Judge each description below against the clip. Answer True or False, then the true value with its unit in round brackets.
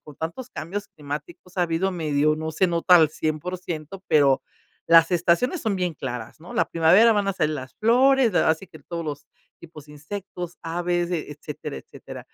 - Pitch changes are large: False (3.3 semitones)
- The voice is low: False (170 Hz)